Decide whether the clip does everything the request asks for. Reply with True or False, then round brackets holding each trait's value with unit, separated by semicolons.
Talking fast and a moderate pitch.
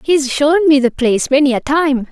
False (225 wpm; 280 Hz)